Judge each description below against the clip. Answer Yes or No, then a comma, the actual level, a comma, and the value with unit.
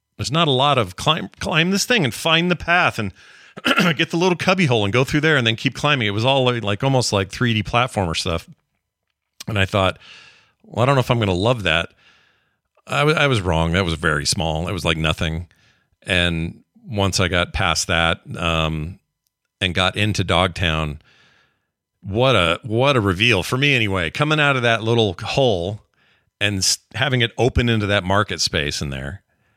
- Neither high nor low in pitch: No, low, 105 Hz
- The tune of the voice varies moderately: No, wide, 6.7 semitones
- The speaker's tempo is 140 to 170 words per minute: No, average, 195 wpm